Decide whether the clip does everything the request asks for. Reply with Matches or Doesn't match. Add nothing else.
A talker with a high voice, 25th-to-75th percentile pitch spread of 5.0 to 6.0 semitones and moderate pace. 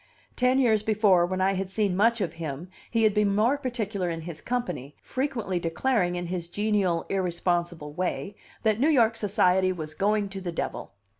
Doesn't match